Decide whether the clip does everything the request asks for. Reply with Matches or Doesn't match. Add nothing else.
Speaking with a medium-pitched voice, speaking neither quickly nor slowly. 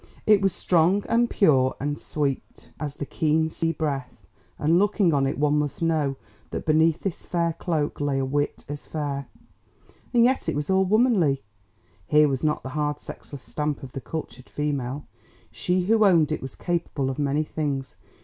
Matches